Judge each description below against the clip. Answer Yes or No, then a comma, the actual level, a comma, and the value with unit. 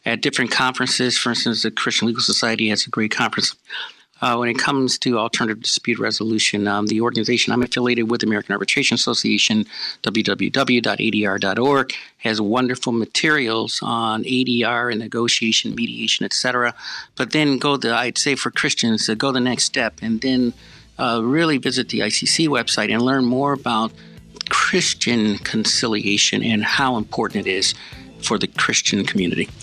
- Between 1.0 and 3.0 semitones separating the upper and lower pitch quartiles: Yes, narrow, 2.4 semitones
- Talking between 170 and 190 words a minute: No, average, 155 wpm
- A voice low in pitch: Yes, low, 120 Hz